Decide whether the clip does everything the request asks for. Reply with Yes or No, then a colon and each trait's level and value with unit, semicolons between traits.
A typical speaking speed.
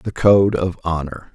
Yes: average, 180 wpm